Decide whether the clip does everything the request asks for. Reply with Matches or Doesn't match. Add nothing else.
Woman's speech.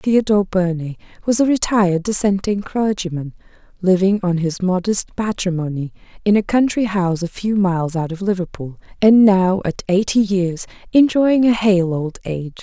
Matches